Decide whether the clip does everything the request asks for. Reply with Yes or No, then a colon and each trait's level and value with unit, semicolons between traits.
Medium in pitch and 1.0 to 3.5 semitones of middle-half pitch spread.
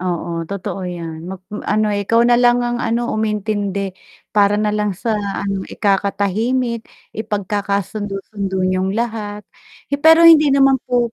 No: high, 210 Hz; average, 3.2 semitones